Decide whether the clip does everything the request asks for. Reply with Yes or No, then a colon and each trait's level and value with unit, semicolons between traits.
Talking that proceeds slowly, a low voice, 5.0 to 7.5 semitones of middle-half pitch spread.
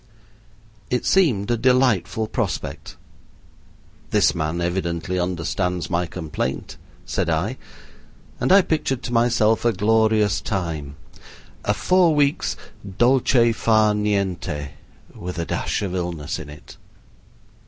Yes: slow, 115 wpm; low, 100 Hz; wide, 5.5 semitones